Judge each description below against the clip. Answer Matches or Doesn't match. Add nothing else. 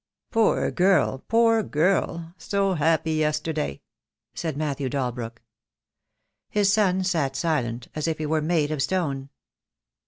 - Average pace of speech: Doesn't match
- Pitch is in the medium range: Matches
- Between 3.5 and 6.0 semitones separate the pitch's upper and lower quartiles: Matches